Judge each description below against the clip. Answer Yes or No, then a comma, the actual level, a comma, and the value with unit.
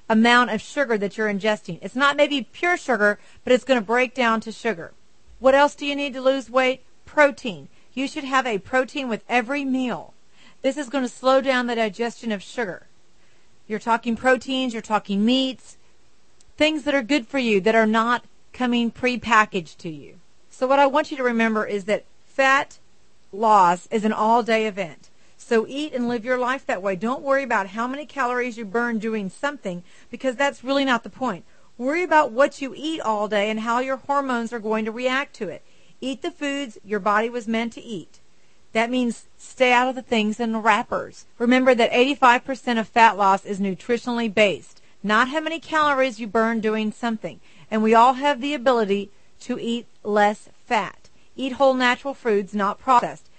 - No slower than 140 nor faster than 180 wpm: No, average, 195 wpm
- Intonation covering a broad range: No, average, 3.5 semitones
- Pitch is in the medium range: No, high, 240 Hz